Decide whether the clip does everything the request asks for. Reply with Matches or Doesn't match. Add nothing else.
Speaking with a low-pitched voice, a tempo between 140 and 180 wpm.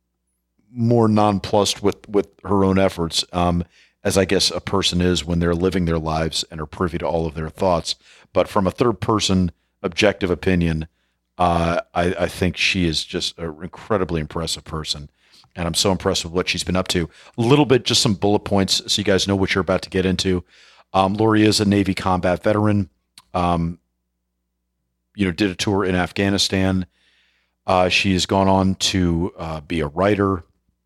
Doesn't match